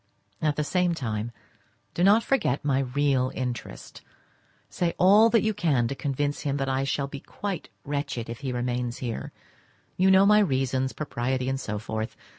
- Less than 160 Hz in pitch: Yes, medium, 140 Hz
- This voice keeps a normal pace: Yes, average, 170 wpm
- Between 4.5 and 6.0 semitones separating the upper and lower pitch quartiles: Yes, average, 5.3 semitones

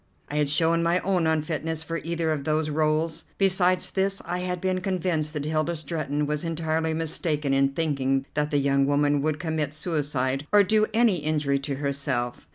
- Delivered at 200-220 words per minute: No, average, 180 wpm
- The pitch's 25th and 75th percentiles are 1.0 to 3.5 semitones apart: Yes, narrow, 2.6 semitones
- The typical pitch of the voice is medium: Yes, medium, 155 Hz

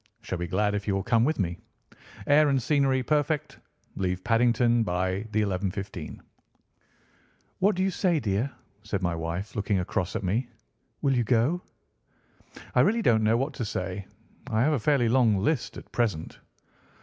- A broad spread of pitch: Yes, wide, 5.8 semitones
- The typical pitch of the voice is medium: No, low, 110 Hz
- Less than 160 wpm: No, average, 170 wpm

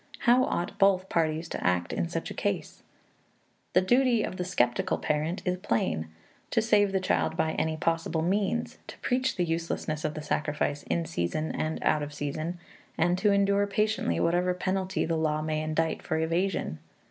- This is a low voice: No, medium, 165 Hz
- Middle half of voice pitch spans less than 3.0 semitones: No, average, 3.8 semitones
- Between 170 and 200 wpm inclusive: Yes, average, 180 wpm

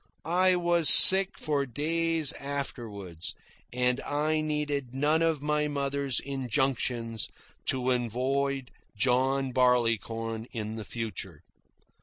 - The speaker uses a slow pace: Yes, slow, 105 wpm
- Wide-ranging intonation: No, average, 3.8 semitones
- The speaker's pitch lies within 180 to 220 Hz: No, low, 135 Hz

